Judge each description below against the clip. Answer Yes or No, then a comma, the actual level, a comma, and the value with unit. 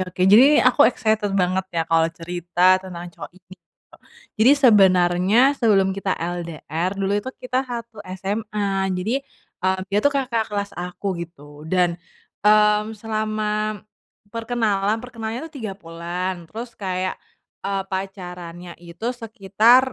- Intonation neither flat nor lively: Yes, average, 3.6 semitones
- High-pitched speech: Yes, high, 195 Hz